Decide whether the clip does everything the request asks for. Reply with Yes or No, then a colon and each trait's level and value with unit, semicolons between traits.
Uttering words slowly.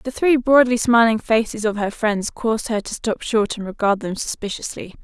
No: fast, 205 wpm